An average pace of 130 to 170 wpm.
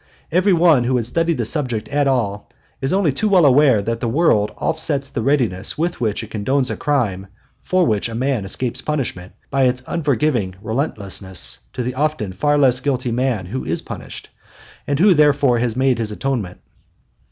No: average, 185 wpm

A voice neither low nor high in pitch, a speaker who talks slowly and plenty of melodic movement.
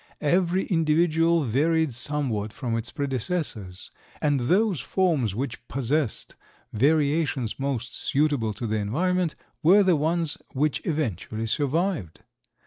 Yes: medium, 145 Hz; slow, 115 wpm; wide, 5.9 semitones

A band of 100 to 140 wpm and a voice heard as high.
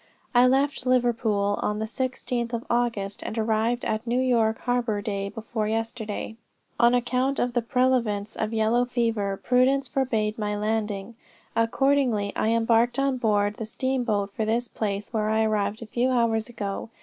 No: average, 160 wpm; high, 230 Hz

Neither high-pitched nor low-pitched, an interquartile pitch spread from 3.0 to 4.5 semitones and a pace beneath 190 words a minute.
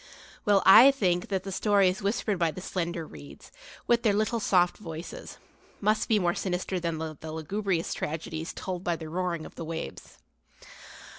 Yes: medium, 180 Hz; average, 3.5 semitones; average, 165 wpm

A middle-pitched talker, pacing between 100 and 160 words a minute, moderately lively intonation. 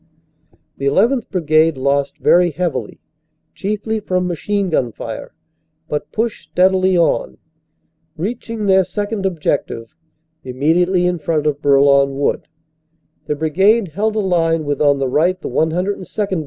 Yes: medium, 175 Hz; average, 140 wpm; average, 4.7 semitones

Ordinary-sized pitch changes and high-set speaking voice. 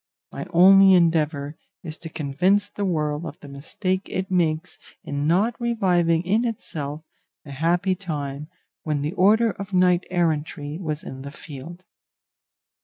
No: average, 3.9 semitones; medium, 170 Hz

